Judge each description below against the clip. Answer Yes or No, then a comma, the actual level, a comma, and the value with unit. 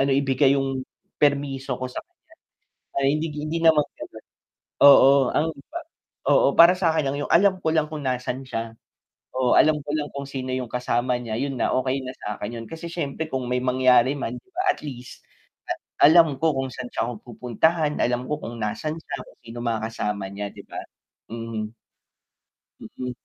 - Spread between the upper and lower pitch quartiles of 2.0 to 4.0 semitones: Yes, average, 3.6 semitones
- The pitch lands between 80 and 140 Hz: Yes, low, 135 Hz